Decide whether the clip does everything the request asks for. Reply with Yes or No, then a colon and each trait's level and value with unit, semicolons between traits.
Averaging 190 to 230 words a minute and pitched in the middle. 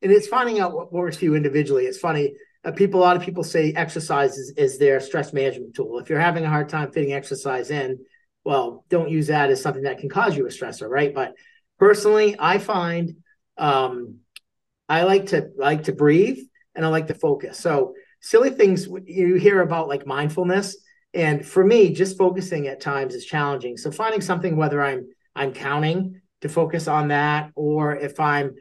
Yes: average, 195 wpm; medium, 165 Hz